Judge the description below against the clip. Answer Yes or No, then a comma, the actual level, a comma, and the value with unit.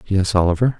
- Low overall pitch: Yes, very low, 95 Hz